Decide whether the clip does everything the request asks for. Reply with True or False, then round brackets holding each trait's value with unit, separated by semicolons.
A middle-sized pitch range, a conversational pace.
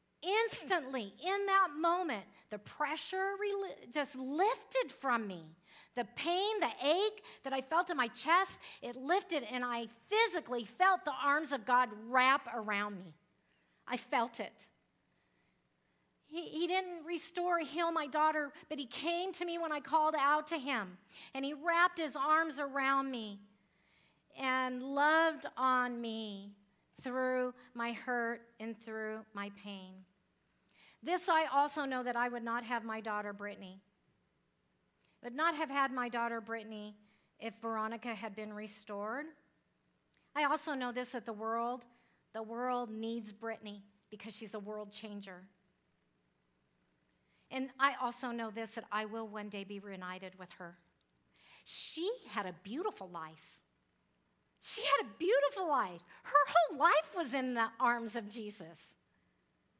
False (6.4 semitones; 145 wpm)